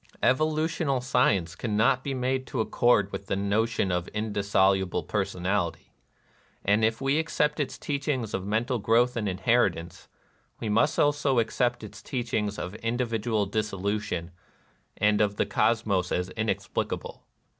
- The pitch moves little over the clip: No, average, 4.1 semitones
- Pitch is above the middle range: No, low, 110 Hz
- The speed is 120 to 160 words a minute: Yes, average, 140 wpm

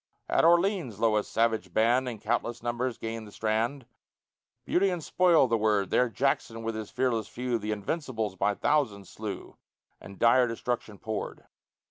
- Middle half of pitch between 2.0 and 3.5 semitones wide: Yes, average, 2.9 semitones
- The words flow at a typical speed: Yes, average, 160 wpm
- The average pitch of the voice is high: No, low, 115 Hz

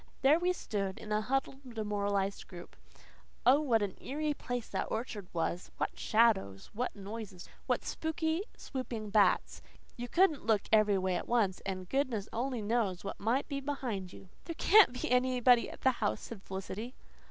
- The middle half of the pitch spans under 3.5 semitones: No, average, 4.8 semitones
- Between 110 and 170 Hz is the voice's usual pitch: No, high, 225 Hz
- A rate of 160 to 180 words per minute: Yes, average, 175 wpm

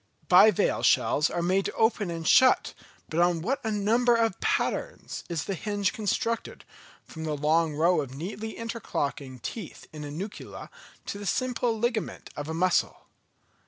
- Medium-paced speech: Yes, average, 160 wpm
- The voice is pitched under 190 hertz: No, high, 195 Hz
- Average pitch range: No, wide, 5.8 semitones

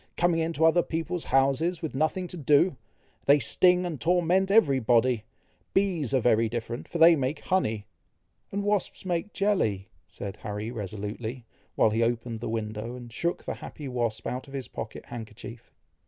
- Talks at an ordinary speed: Yes, average, 170 wpm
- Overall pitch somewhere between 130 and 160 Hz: Yes, low, 135 Hz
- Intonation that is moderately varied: No, wide, 6.9 semitones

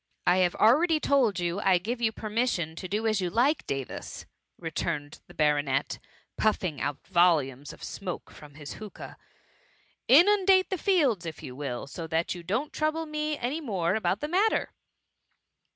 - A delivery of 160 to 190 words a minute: Yes, average, 175 wpm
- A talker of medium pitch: No, high, 195 Hz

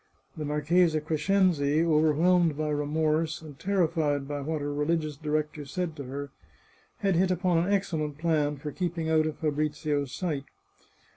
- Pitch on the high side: No, medium, 155 Hz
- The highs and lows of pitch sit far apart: No, narrow, 2.4 semitones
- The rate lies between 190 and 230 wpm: No, average, 150 wpm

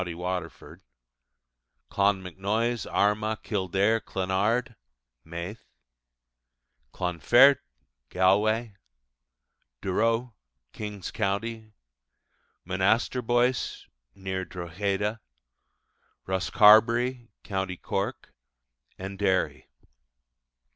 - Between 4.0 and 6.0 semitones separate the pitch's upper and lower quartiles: No, average, 3.3 semitones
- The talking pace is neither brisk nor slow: No, slow, 55 wpm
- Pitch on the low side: Yes, low, 100 Hz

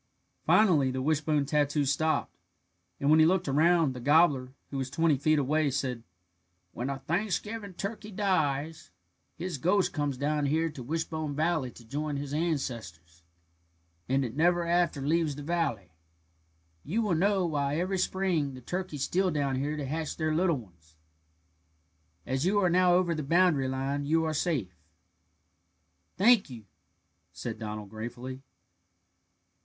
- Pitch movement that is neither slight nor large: Yes, average, 4.2 semitones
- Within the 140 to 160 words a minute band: Yes, average, 150 wpm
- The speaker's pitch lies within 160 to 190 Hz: No, medium, 150 Hz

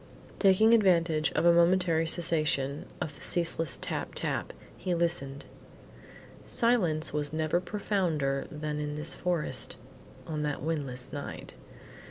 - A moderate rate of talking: No, slow, 125 wpm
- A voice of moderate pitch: Yes, medium, 160 Hz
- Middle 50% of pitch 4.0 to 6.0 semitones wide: No, average, 2.8 semitones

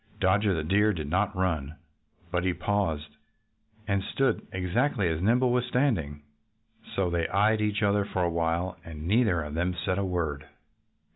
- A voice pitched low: Yes, very low, 95 Hz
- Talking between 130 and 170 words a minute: Yes, average, 165 wpm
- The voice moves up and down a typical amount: Yes, average, 3.9 semitones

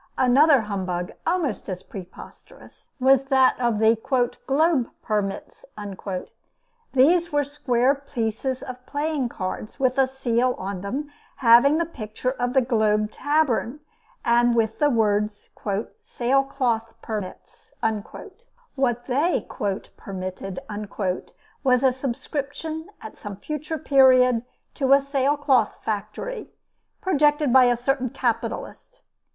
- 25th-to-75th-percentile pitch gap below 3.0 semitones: No, average, 4.1 semitones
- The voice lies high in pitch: Yes, very high, 255 Hz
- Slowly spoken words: Yes, slow, 110 wpm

